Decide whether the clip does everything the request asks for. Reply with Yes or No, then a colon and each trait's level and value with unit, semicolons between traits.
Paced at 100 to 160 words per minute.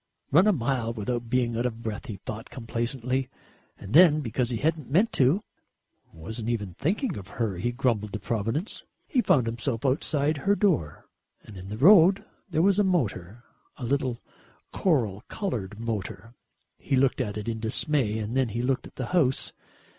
No: average, 175 wpm